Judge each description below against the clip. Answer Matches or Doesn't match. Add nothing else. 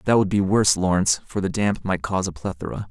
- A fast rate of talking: Matches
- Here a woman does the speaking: Doesn't match